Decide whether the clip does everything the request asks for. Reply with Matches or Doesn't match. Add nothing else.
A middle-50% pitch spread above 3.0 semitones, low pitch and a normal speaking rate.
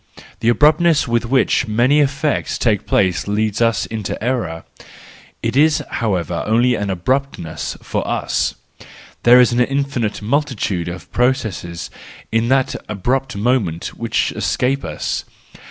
Doesn't match